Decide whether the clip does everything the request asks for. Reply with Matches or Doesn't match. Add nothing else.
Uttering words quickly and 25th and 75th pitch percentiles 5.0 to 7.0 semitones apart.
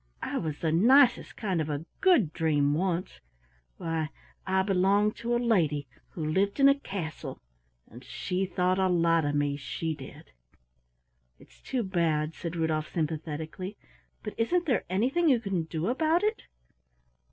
Doesn't match